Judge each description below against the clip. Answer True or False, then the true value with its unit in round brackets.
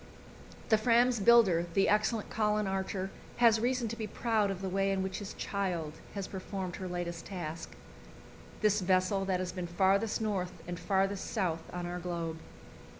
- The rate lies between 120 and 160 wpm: False (170 wpm)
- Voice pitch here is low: False (195 Hz)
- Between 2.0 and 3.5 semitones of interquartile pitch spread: True (2.9 semitones)